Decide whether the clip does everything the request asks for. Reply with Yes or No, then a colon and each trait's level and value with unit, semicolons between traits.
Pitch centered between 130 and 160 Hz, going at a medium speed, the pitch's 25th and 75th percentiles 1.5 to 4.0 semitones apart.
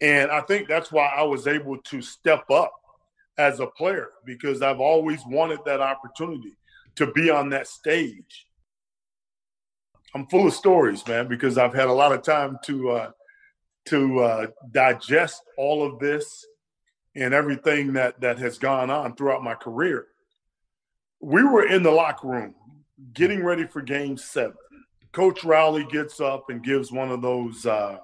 Yes: medium, 140 Hz; average, 165 wpm; average, 3.3 semitones